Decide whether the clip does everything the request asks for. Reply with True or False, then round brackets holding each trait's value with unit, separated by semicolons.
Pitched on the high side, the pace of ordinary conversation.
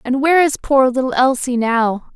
True (260 Hz; 195 wpm)